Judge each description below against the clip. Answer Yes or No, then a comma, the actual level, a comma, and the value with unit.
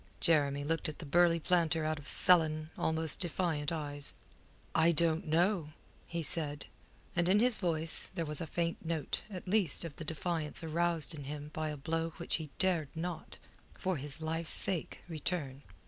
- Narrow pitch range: Yes, narrow, 2.2 semitones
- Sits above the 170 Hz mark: No, medium, 160 Hz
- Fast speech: No, average, 175 wpm